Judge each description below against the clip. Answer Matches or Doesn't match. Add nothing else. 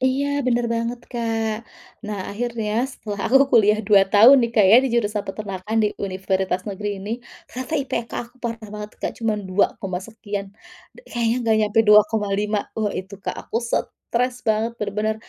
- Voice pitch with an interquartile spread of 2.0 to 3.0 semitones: Matches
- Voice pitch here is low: Doesn't match